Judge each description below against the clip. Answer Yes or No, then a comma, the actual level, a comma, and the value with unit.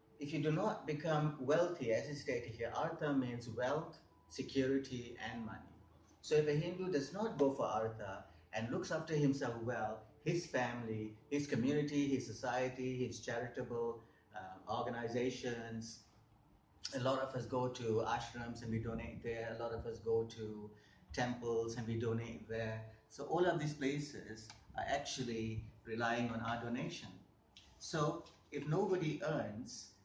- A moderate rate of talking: Yes, average, 155 wpm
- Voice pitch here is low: Yes, low, 120 Hz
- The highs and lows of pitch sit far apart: No, average, 4.1 semitones